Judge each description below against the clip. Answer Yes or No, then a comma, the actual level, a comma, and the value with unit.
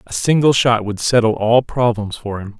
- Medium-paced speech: No, fast, 210 wpm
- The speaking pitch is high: No, low, 115 Hz